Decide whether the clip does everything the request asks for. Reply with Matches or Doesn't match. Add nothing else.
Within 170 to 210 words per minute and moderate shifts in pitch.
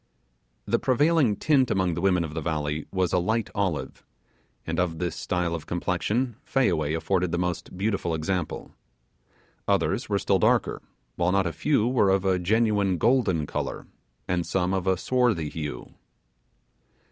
Doesn't match